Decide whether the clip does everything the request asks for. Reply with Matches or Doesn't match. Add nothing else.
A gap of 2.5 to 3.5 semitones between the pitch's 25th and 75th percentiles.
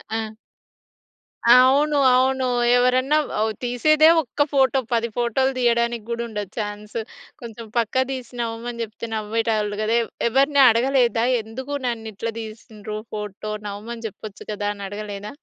Matches